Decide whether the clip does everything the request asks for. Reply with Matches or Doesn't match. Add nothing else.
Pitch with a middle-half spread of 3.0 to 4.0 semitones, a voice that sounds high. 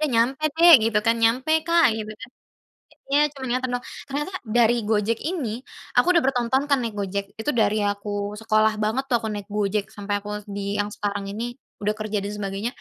Matches